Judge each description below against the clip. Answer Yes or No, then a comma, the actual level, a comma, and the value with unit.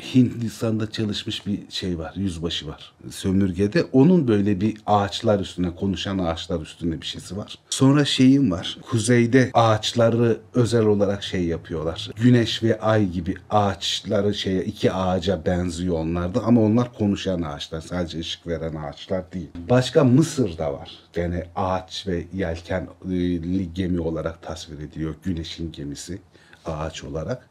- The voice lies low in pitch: Yes, very low, 95 Hz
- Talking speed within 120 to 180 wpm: Yes, average, 135 wpm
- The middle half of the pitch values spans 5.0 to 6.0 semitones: No, average, 4.4 semitones